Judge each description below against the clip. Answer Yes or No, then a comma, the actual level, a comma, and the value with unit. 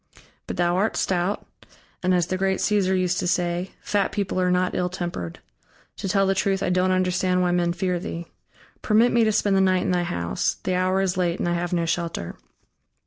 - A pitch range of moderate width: No, narrow, 1.5 semitones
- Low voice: No, medium, 185 Hz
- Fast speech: Yes, fast, 215 wpm